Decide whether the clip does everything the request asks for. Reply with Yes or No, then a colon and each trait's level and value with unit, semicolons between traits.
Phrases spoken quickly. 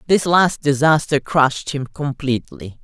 No: slow, 125 wpm